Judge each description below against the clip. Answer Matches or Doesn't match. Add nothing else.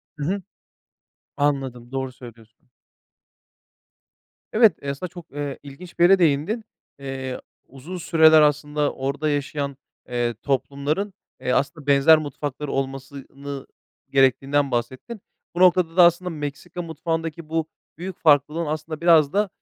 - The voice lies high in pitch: Doesn't match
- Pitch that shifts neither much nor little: Matches